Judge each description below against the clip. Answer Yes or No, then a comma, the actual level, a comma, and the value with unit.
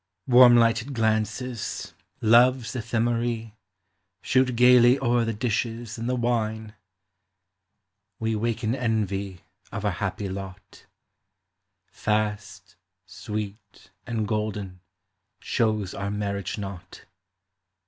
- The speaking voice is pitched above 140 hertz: No, low, 110 Hz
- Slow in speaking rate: Yes, slow, 95 wpm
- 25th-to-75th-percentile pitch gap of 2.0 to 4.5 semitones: Yes, narrow, 2.6 semitones